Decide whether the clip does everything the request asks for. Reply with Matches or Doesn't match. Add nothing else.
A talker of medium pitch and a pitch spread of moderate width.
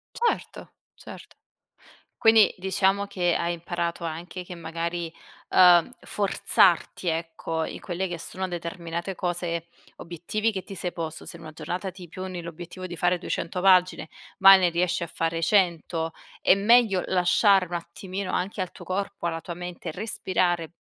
Doesn't match